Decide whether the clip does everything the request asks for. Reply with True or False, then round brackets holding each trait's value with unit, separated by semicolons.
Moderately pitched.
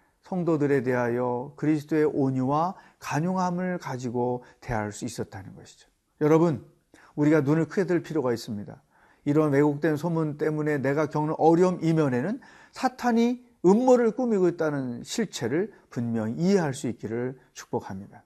True (150 Hz)